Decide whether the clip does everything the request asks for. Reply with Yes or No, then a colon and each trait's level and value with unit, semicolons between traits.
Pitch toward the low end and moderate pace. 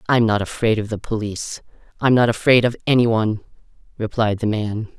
Yes: low, 110 Hz; average, 155 wpm